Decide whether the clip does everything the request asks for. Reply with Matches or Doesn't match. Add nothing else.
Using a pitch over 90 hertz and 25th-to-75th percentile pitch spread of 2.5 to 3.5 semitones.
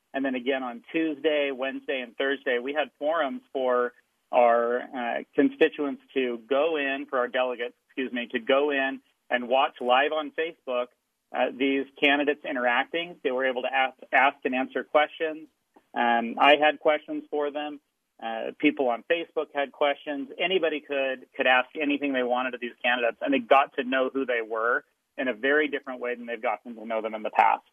Matches